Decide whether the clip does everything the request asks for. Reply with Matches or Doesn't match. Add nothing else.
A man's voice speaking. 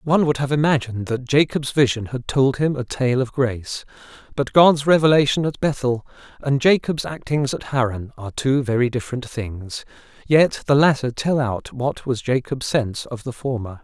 Matches